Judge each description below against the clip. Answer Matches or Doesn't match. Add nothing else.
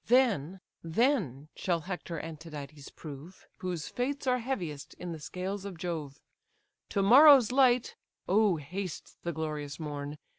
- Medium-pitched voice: Matches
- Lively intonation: Matches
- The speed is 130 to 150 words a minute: Matches